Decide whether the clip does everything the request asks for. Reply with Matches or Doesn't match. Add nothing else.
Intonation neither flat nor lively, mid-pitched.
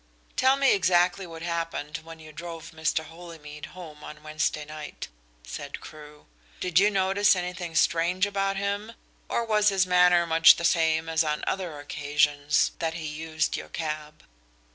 Matches